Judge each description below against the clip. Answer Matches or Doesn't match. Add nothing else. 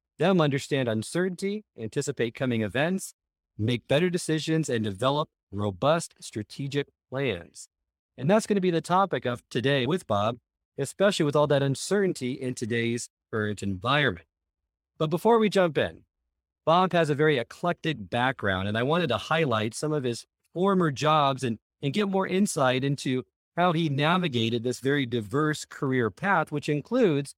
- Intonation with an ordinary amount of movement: Doesn't match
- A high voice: Doesn't match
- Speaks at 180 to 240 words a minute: Doesn't match